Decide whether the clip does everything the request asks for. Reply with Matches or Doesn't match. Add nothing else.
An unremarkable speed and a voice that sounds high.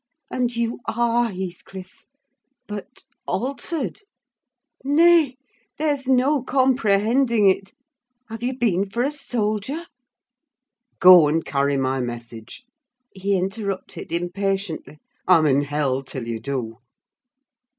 Doesn't match